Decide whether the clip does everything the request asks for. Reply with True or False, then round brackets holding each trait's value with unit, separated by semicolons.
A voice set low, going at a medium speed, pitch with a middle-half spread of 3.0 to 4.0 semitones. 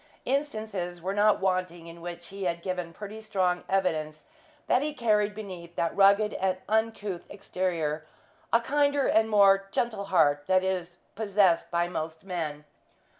False (190 Hz; 150 wpm; 3.5 semitones)